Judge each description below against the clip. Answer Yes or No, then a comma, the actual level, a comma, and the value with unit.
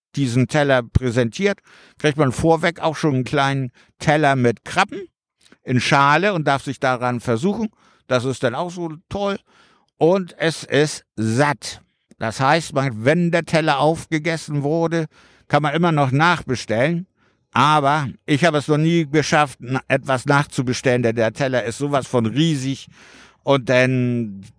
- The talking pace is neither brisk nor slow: Yes, average, 145 wpm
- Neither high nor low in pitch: Yes, medium, 145 Hz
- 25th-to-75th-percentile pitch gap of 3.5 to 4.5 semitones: Yes, average, 4.0 semitones